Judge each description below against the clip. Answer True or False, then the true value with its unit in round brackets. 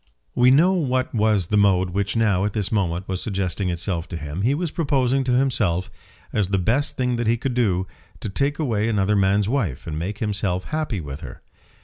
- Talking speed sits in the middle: False (210 wpm)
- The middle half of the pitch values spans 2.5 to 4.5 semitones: False (5.1 semitones)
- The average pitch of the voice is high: False (105 Hz)